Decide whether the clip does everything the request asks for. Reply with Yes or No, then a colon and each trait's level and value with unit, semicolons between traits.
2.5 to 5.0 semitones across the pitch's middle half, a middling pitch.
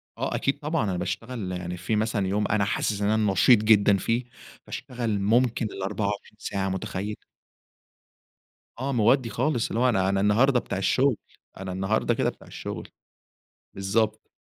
No: average, 3.3 semitones; low, 105 Hz